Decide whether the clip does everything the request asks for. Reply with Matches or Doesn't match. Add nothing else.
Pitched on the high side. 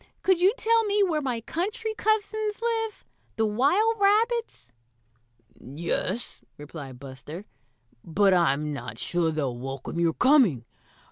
Matches